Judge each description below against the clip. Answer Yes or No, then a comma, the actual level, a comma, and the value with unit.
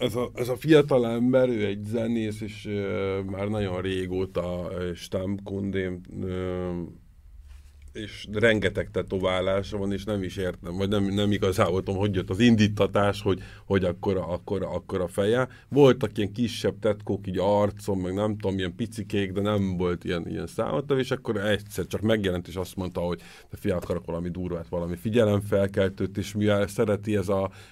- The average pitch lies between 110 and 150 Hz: No, low, 100 Hz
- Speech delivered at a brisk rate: Yes, fast, 165 wpm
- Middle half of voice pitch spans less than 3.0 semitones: Yes, narrow, 2.4 semitones